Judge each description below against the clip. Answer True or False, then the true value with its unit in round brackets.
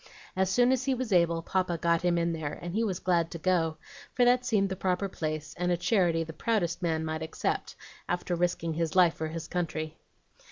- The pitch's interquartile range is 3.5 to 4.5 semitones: False (2.5 semitones)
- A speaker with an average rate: False (215 wpm)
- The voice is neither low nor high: True (175 Hz)